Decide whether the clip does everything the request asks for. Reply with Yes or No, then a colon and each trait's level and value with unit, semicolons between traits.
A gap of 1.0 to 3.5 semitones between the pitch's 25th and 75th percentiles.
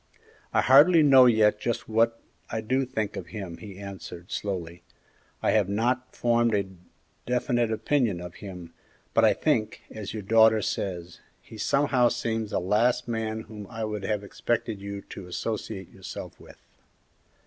Yes: average, 3.1 semitones